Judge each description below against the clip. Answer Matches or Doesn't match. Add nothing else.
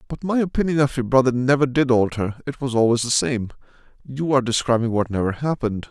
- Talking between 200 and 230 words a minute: Matches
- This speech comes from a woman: Doesn't match